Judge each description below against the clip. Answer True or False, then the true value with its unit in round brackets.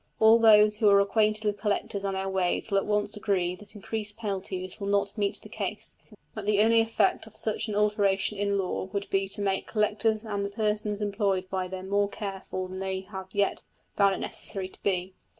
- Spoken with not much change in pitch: True (1.6 semitones)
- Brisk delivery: True (215 wpm)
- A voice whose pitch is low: False (200 Hz)